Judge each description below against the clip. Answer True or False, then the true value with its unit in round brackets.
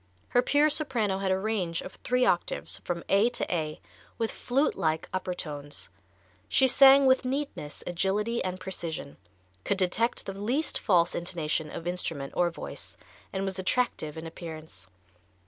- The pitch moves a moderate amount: False (6.1 semitones)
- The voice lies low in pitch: False (185 Hz)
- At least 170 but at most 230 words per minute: False (155 wpm)